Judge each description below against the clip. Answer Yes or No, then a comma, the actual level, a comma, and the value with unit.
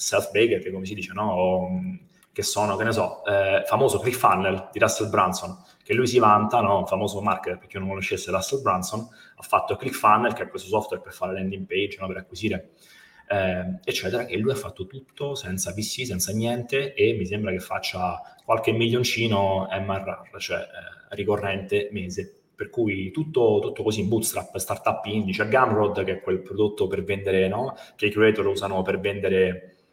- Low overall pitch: Yes, low, 100 Hz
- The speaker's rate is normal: No, fast, 185 wpm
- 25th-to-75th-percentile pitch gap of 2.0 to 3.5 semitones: Yes, average, 2.9 semitones